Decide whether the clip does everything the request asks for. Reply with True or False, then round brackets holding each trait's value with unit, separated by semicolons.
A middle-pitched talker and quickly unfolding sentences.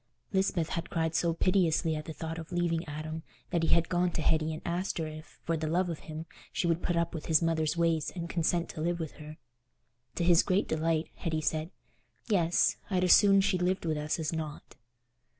True (165 Hz; 220 wpm)